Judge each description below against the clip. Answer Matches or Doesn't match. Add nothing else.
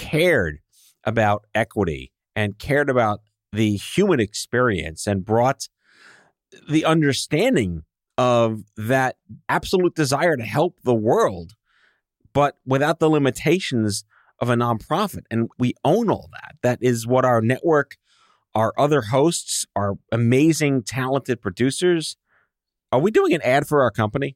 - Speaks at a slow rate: Matches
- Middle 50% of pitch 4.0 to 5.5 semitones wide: Matches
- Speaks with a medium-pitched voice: Doesn't match